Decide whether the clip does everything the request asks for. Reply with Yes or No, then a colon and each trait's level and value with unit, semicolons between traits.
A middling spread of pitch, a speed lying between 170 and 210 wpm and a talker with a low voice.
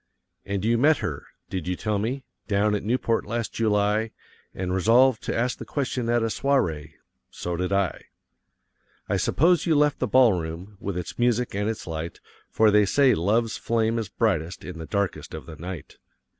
Yes: average, 4.5 semitones; average, 185 wpm; low, 105 Hz